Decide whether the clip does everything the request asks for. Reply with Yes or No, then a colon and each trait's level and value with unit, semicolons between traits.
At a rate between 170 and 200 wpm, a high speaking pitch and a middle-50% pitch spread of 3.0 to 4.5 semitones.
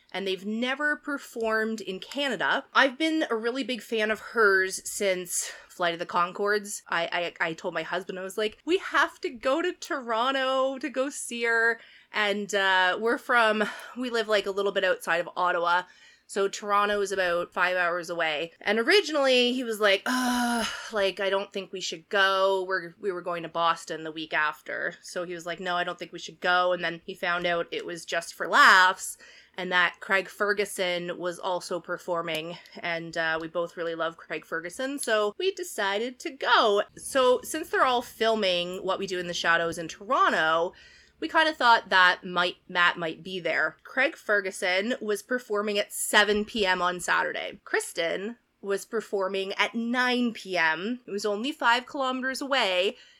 No: average, 185 wpm; high, 195 Hz; average, 5.1 semitones